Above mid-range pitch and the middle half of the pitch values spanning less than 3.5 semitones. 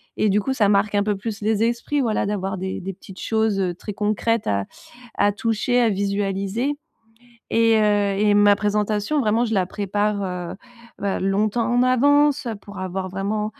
Yes: high, 210 Hz; narrow, 2.4 semitones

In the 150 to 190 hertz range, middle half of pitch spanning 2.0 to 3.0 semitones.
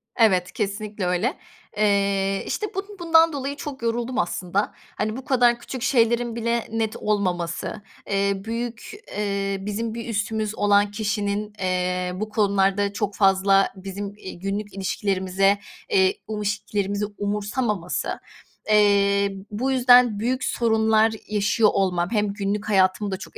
No: high, 210 Hz; narrow, 2.6 semitones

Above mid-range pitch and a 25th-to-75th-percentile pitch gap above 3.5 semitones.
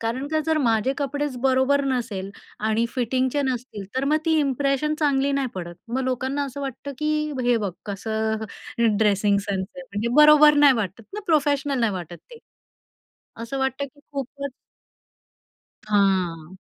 Yes: very high, 260 Hz; average, 4.6 semitones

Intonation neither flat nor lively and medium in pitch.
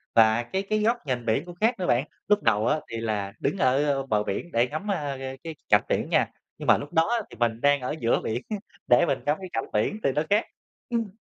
No: wide, 7.9 semitones; medium, 145 Hz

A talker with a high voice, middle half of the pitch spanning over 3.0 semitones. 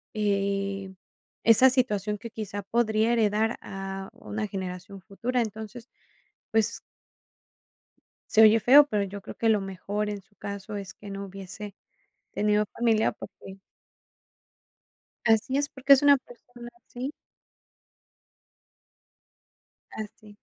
No: high, 210 Hz; average, 2.7 semitones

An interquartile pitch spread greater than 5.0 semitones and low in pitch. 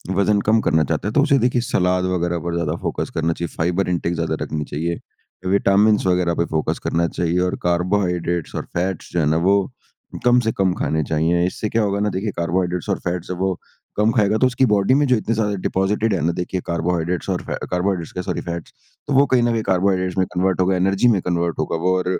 No: average, 3.1 semitones; very low, 90 Hz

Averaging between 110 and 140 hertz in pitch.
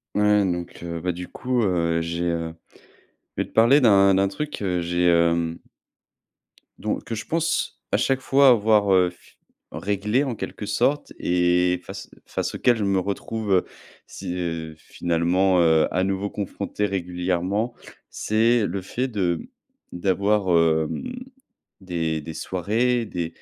No: very low, 95 Hz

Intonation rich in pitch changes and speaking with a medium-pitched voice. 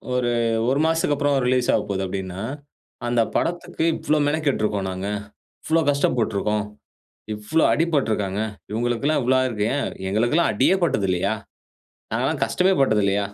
No: wide, 6.0 semitones; low, 120 Hz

